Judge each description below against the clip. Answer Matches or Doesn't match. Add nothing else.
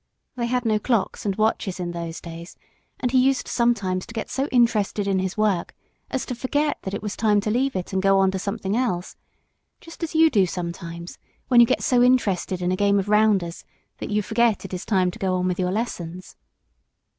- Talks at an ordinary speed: Doesn't match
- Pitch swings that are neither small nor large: Matches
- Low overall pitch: Doesn't match